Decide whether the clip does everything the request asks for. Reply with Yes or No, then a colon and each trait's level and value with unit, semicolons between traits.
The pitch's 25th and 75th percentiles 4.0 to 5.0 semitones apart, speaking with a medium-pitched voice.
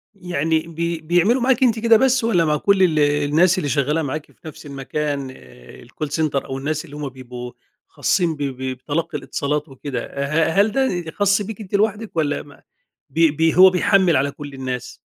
Yes: average, 4.5 semitones; medium, 155 Hz